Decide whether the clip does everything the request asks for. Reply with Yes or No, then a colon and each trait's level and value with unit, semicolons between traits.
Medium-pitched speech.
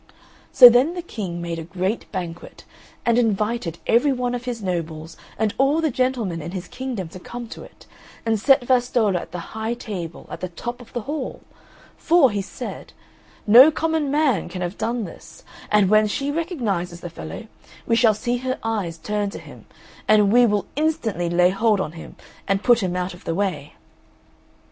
No: high, 215 Hz